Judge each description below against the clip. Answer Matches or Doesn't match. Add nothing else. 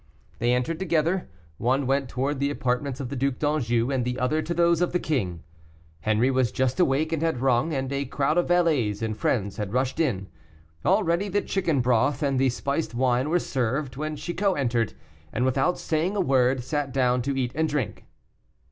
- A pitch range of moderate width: Matches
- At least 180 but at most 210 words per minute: Matches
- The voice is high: Doesn't match